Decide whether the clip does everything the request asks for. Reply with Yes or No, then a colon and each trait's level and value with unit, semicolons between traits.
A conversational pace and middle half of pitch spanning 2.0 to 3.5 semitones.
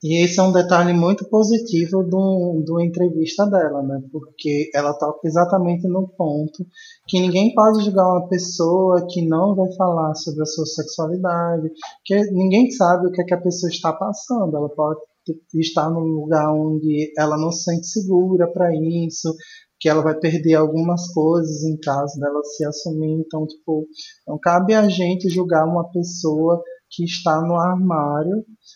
Yes: average, 165 wpm; average, 2.8 semitones